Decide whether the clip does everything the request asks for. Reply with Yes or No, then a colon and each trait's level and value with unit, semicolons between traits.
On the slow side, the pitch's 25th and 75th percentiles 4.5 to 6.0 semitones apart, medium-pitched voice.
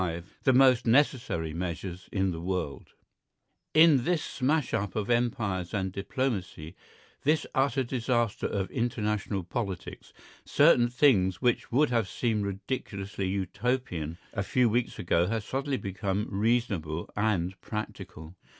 No: slow, 130 wpm; average, 4.9 semitones; low, 105 Hz